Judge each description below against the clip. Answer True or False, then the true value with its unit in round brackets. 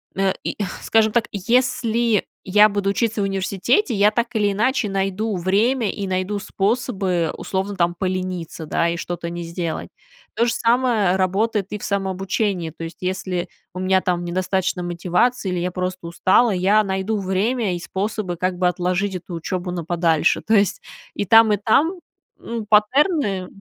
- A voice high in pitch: True (195 Hz)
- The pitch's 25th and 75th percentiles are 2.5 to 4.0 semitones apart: True (3.1 semitones)